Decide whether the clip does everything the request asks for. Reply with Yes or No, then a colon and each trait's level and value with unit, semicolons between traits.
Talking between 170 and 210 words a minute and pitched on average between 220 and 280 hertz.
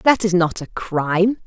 No: fast, 205 wpm; medium, 185 Hz